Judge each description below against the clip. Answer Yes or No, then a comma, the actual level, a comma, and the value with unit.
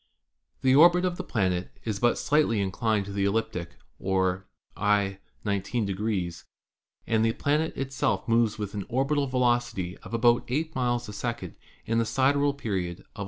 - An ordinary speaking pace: Yes, average, 165 wpm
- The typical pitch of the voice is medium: No, low, 115 Hz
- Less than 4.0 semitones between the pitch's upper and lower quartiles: No, average, 4.7 semitones